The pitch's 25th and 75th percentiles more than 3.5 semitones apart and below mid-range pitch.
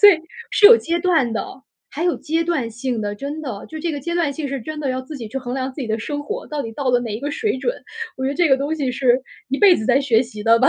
No: average, 4.3 semitones; very high, 275 Hz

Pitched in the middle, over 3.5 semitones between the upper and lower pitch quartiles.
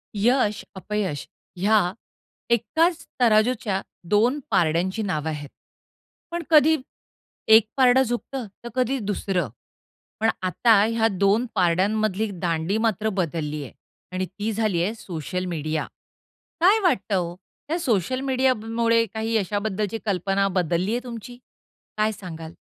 No: high, 210 Hz; average, 4.3 semitones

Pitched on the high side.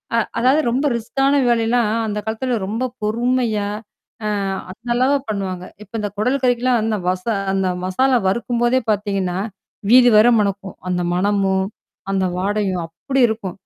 Yes: high, 220 Hz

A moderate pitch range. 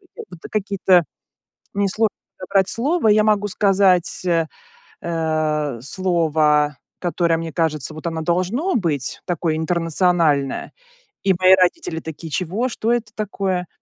Yes: average, 3.7 semitones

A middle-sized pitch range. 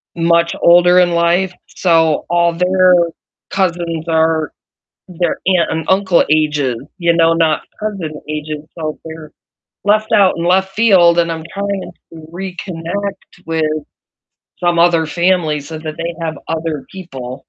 No: narrow, 2.2 semitones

